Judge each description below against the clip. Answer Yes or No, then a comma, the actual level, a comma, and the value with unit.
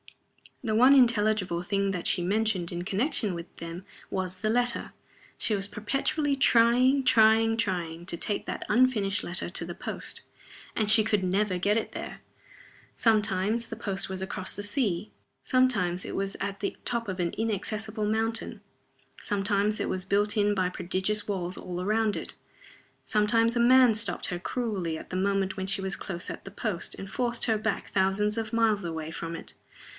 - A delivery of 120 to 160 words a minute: No, average, 175 wpm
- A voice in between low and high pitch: No, high, 205 Hz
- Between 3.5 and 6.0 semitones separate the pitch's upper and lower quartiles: No, average, 3.1 semitones